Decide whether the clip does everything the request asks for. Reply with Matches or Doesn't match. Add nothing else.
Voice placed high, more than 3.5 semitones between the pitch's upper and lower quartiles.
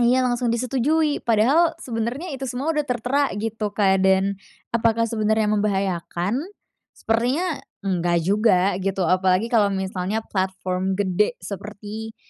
Matches